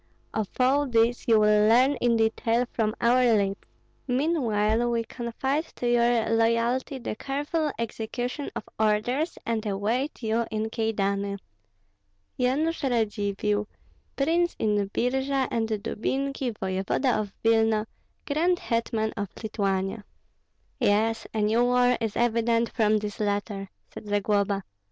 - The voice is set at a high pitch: Yes, high, 230 Hz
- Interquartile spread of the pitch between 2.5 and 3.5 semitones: Yes, average, 2.9 semitones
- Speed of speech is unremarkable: No, slow, 125 wpm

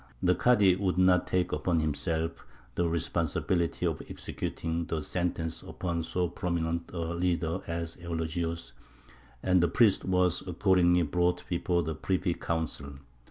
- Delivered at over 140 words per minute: No, slow, 135 wpm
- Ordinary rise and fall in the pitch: No, narrow, 1.7 semitones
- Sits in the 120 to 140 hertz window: No, very low, 85 Hz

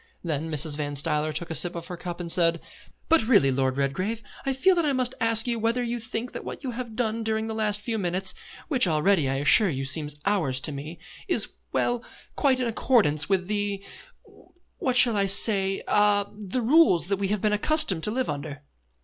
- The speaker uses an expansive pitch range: Yes, wide, 6.1 semitones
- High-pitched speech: Yes, high, 200 Hz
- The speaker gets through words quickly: Yes, fast, 215 wpm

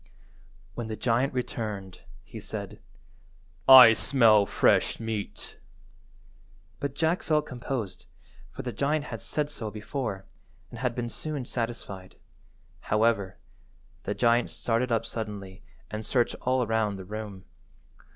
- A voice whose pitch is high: No, low, 115 Hz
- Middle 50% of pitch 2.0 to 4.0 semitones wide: Yes, average, 3.2 semitones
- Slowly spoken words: Yes, slow, 125 wpm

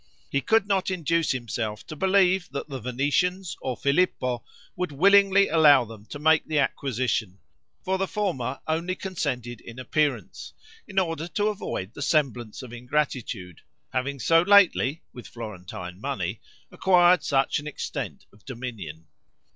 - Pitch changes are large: Yes, wide, 6.8 semitones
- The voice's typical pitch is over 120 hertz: Yes, medium, 140 Hz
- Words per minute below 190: Yes, average, 145 wpm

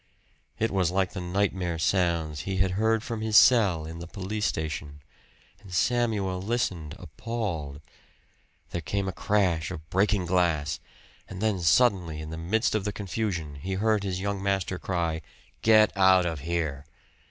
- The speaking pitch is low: Yes, very low, 95 Hz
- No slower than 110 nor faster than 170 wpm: Yes, average, 160 wpm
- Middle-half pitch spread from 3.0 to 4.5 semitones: Yes, average, 3.9 semitones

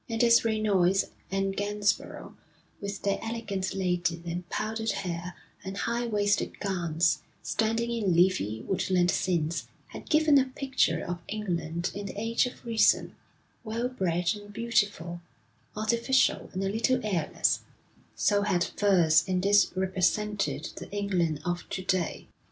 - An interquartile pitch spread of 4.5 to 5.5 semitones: No, average, 3.8 semitones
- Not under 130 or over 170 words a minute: Yes, average, 140 wpm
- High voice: Yes, high, 200 Hz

